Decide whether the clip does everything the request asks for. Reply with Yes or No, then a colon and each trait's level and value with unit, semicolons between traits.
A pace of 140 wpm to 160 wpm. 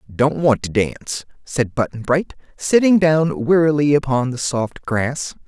Yes: average, 155 wpm